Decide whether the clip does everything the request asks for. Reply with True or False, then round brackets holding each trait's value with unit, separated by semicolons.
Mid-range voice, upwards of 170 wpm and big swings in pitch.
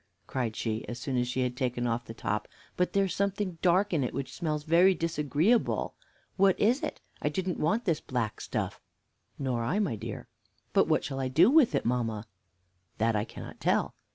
True (145 Hz; 195 wpm; 7.3 semitones)